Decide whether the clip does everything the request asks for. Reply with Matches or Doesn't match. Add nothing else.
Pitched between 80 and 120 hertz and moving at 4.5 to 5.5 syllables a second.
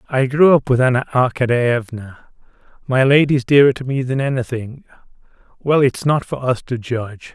Doesn't match